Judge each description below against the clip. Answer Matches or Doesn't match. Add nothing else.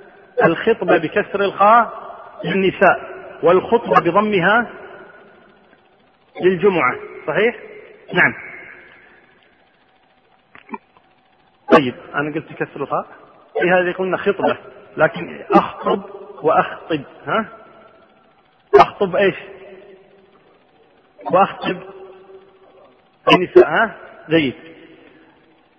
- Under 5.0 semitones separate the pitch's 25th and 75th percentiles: Matches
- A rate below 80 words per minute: Matches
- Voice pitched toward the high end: Matches